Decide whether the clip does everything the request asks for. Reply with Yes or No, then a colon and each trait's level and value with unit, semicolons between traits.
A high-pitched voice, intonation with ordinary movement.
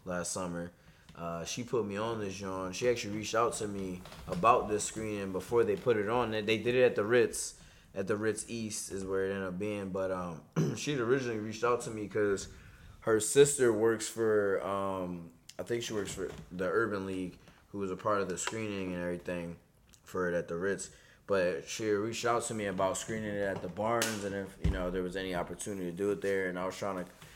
No: low, 100 Hz; average, 3.0 semitones